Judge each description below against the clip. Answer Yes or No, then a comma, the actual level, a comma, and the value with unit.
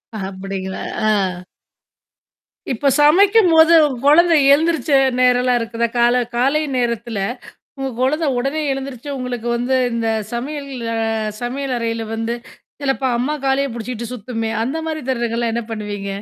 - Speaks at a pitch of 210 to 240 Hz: No, very high, 250 Hz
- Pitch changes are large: No, average, 3.7 semitones